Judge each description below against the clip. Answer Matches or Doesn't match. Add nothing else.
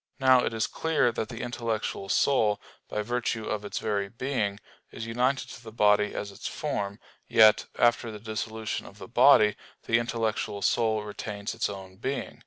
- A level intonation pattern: Matches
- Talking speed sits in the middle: Matches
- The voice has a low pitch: Matches